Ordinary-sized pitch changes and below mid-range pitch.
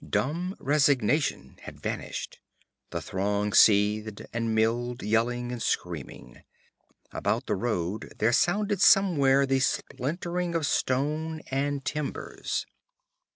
No: wide, 5.7 semitones; low, 130 Hz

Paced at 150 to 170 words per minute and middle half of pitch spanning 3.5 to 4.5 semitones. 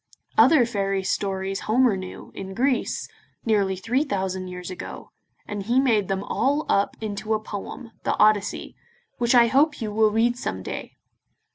Yes: average, 160 wpm; average, 3.8 semitones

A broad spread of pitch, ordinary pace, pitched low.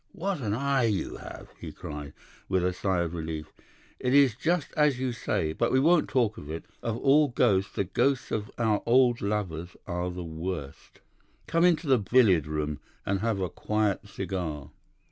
Yes: wide, 6.9 semitones; average, 185 wpm; low, 105 Hz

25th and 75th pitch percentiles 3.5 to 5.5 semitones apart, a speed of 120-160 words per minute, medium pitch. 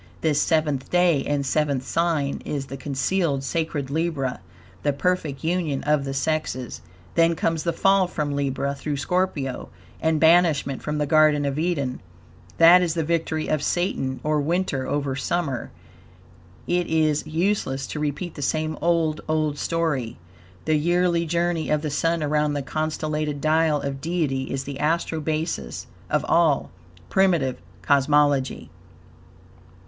No: average, 2.9 semitones; average, 145 wpm; medium, 155 Hz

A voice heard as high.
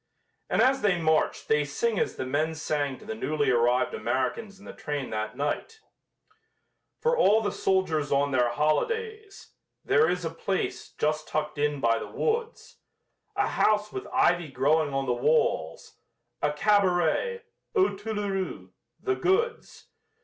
No: medium, 160 Hz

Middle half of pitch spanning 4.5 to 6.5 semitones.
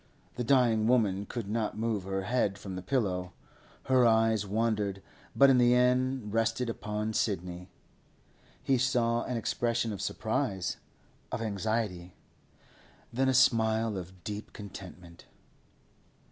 No: average, 3.7 semitones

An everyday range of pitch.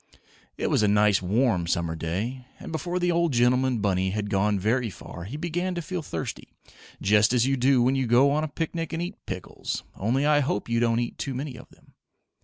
No: wide, 6.0 semitones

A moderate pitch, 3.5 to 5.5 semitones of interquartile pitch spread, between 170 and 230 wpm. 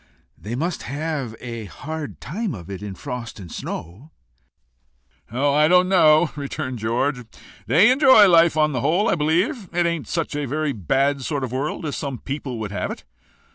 Yes: medium, 145 Hz; average, 5.0 semitones; average, 185 wpm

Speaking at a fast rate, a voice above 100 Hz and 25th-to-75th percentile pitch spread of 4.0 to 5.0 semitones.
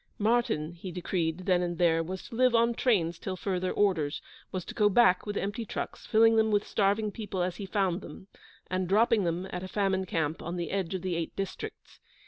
No: fast, 215 wpm; high, 190 Hz; average, 3.1 semitones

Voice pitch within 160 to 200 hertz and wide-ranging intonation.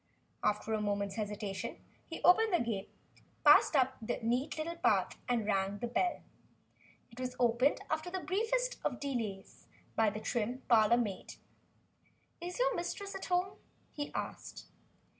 No: high, 245 Hz; wide, 8.5 semitones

